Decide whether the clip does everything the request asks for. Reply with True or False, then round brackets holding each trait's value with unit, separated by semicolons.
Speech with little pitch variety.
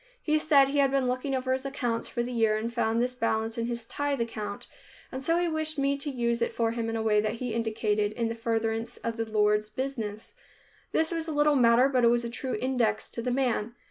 False (3.1 semitones)